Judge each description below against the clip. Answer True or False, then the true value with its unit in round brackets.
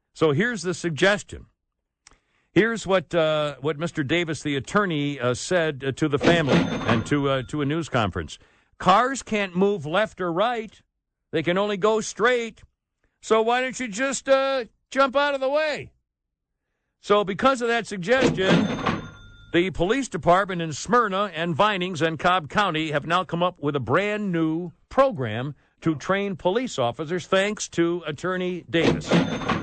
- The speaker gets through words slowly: False (160 wpm)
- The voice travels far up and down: True (5.7 semitones)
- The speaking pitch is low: False (180 Hz)